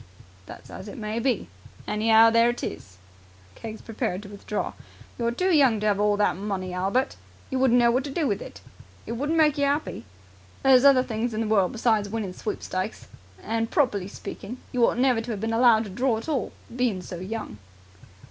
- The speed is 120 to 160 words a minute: No, average, 200 wpm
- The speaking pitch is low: No, high, 225 Hz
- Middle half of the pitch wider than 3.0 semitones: Yes, average, 3.4 semitones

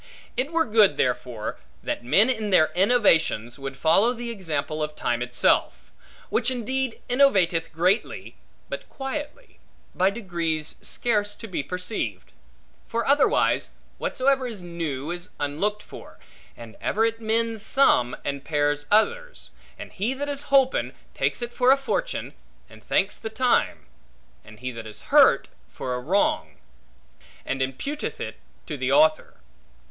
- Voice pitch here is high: Yes, high, 205 Hz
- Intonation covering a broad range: Yes, wide, 9.0 semitones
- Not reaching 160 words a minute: Yes, average, 145 wpm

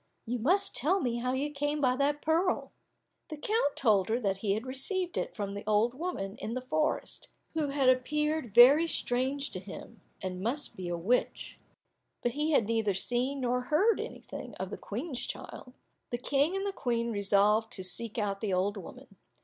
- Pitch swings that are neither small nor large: No, wide, 5.7 semitones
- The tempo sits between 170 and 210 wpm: Yes, average, 190 wpm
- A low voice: No, very high, 250 Hz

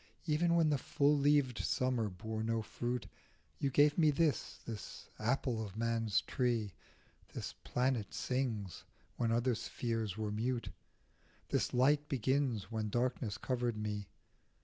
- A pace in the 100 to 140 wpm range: Yes, slow, 135 wpm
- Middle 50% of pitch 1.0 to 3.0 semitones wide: No, average, 3.6 semitones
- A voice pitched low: Yes, low, 120 Hz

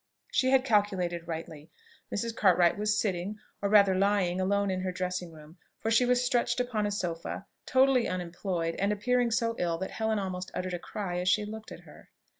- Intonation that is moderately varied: Yes, average, 3.7 semitones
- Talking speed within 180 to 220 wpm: Yes, average, 195 wpm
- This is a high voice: Yes, high, 200 Hz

